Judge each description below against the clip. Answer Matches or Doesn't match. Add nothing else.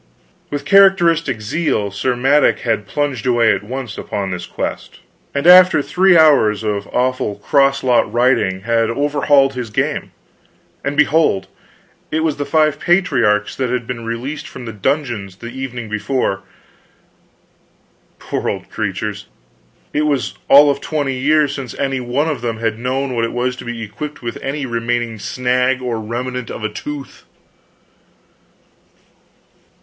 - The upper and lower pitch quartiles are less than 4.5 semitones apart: Matches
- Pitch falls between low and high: Doesn't match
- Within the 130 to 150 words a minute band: Matches